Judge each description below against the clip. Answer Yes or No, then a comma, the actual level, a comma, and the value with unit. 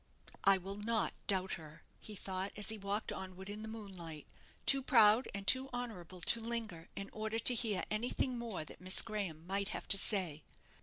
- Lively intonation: No, average, 3.2 semitones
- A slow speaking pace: No, average, 190 wpm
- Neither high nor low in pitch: No, high, 200 Hz